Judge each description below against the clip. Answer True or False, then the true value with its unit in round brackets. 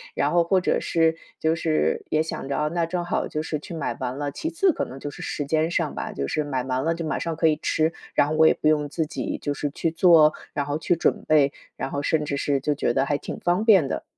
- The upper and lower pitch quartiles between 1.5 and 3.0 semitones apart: True (2.5 semitones)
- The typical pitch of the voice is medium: True (155 Hz)